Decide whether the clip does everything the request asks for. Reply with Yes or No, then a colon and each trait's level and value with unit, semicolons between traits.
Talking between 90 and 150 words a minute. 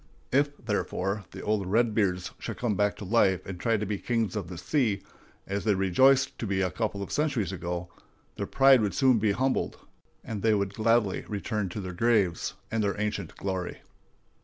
No: average, 190 wpm